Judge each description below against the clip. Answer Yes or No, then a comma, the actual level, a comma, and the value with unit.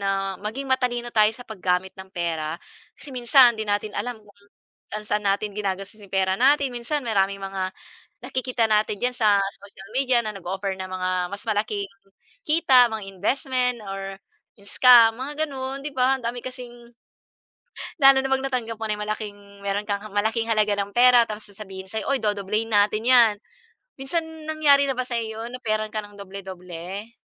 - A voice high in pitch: Yes, high, 215 Hz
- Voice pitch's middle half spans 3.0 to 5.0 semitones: Yes, average, 3.9 semitones